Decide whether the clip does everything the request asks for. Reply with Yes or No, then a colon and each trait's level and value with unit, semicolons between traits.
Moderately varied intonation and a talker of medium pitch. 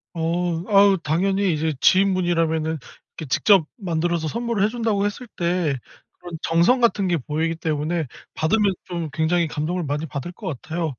Yes: average, 3.4 semitones; medium, 170 Hz